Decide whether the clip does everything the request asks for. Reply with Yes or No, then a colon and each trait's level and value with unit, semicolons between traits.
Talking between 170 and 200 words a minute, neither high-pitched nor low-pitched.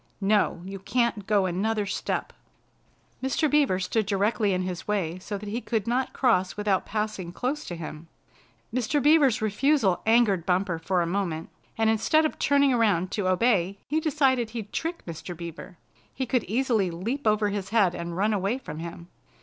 No: average, 175 wpm; high, 205 Hz